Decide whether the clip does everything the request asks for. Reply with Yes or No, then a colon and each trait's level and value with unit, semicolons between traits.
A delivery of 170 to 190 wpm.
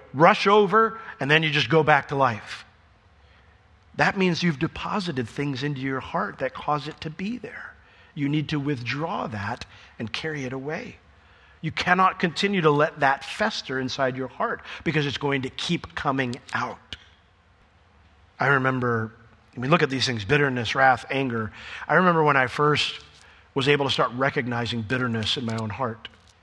Yes: average, 175 wpm